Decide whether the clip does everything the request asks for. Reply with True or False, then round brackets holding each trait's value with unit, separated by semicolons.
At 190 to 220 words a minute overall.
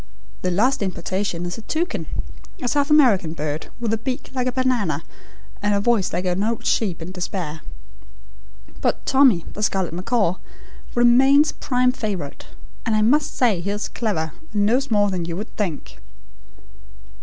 False (165 wpm)